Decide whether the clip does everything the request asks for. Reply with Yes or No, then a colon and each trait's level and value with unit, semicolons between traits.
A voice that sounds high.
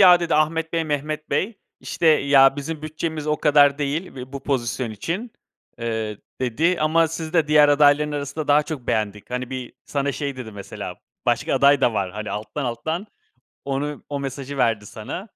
No: medium, 145 Hz